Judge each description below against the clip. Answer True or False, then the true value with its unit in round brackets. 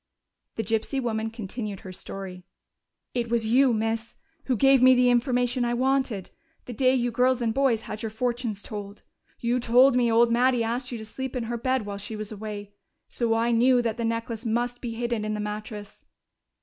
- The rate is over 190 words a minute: True (200 wpm)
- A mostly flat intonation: True (2.2 semitones)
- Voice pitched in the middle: False (235 Hz)